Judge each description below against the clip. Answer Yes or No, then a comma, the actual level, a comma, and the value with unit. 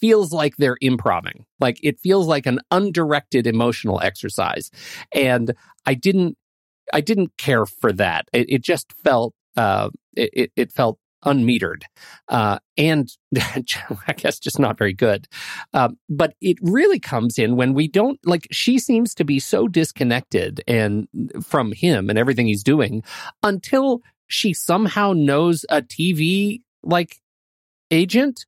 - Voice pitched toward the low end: No, medium, 155 Hz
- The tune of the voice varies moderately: No, wide, 7.3 semitones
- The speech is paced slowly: No, average, 145 wpm